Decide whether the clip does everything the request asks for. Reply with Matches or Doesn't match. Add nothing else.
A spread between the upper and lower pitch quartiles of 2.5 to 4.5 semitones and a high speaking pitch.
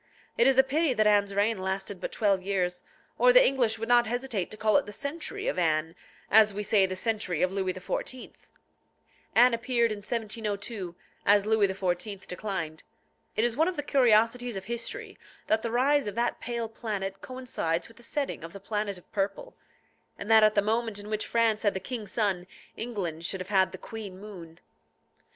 Matches